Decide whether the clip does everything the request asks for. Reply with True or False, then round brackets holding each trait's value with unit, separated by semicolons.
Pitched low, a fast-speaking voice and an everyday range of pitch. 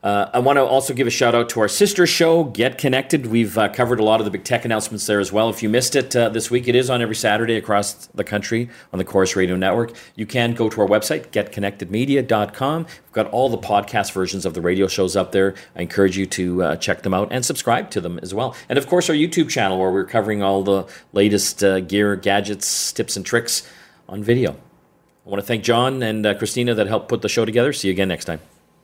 True (110 Hz; 250 wpm; 3.8 semitones)